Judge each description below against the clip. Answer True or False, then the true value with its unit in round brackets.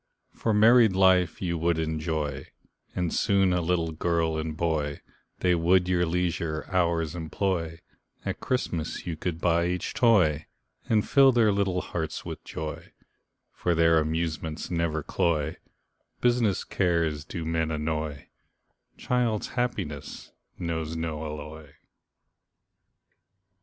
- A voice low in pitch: True (85 Hz)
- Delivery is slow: True (120 wpm)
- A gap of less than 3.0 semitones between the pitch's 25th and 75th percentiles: True (2.5 semitones)